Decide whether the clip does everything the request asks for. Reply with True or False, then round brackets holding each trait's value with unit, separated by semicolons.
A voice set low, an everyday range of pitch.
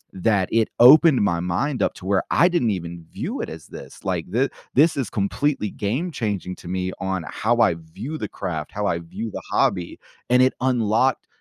False (105 Hz; 5.8 semitones)